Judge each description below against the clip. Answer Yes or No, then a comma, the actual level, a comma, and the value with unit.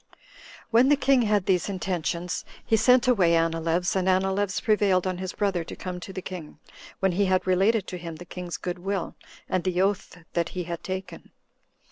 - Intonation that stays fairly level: Yes, narrow, 2.1 semitones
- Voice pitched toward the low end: No, medium, 185 Hz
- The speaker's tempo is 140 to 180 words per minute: No, average, 195 wpm